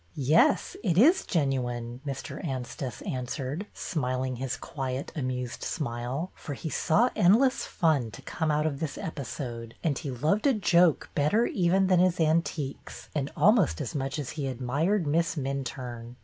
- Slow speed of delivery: No, average, 165 wpm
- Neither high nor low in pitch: Yes, medium, 145 Hz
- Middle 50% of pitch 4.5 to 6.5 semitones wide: Yes, average, 4.9 semitones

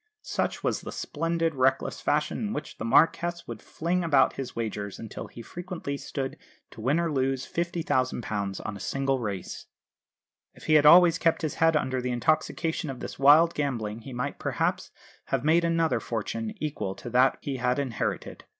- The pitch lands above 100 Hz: Yes, medium, 140 Hz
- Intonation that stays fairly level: No, average, 5.1 semitones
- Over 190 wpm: No, average, 180 wpm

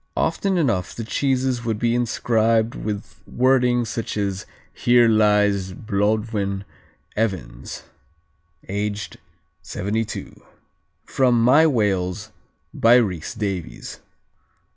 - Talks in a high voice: No, low, 110 Hz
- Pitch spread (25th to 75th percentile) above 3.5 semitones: No, average, 3.2 semitones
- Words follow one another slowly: Yes, slow, 95 wpm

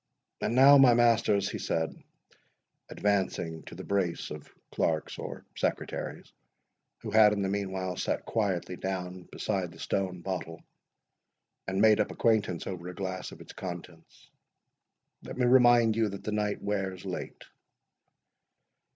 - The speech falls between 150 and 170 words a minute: No, average, 140 wpm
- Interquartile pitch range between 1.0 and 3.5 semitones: Yes, average, 3.0 semitones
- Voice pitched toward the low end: Yes, very low, 95 Hz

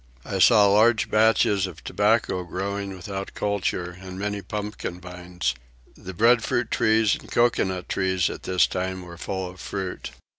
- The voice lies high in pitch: No, very low, 95 Hz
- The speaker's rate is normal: Yes, average, 150 wpm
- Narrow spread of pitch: Yes, narrow, 2.3 semitones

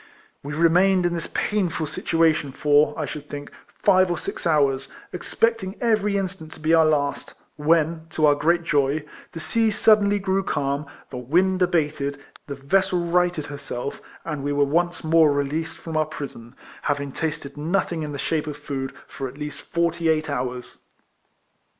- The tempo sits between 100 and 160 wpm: No, average, 170 wpm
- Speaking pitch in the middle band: Yes, medium, 155 Hz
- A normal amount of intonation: Yes, average, 3.4 semitones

